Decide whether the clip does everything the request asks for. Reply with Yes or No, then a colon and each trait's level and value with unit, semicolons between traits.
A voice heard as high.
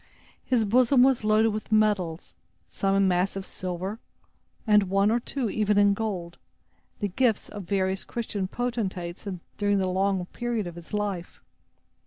Yes: high, 205 Hz